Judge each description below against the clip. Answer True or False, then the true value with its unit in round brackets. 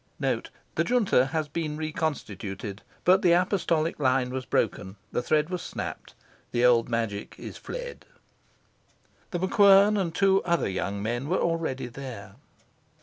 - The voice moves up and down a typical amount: False (6.8 semitones)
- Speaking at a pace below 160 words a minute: True (140 wpm)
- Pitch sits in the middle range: True (155 Hz)